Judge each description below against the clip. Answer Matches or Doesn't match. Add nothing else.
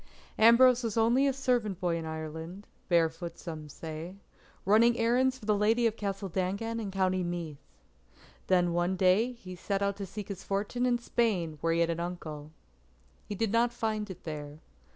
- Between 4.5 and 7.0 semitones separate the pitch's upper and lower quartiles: Matches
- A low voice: Doesn't match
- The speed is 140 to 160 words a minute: Doesn't match